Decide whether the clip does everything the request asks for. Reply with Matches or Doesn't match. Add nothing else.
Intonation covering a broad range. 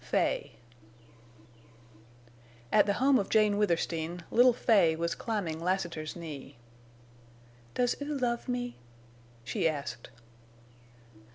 Matches